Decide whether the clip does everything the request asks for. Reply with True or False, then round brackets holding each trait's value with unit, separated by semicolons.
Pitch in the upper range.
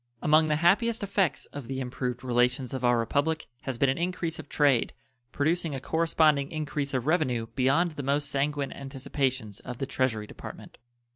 False (140 Hz)